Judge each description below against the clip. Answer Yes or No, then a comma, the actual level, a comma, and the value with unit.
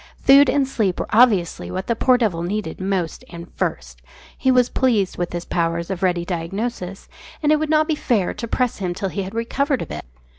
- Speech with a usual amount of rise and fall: No, wide, 6.2 semitones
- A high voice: Yes, high, 200 Hz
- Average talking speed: No, fast, 215 wpm